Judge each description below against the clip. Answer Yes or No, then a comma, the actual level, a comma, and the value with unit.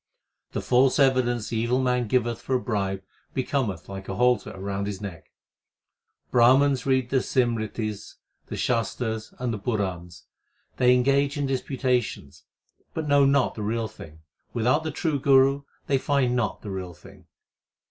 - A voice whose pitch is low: Yes, low, 125 Hz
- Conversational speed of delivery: Yes, average, 155 wpm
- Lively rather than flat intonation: No, average, 4.1 semitones